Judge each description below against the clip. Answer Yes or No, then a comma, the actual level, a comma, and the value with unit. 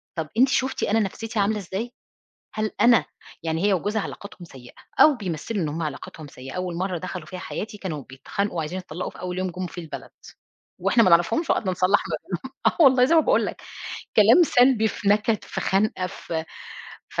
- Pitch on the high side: Yes, high, 195 Hz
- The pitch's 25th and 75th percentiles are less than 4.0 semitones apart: No, average, 4.5 semitones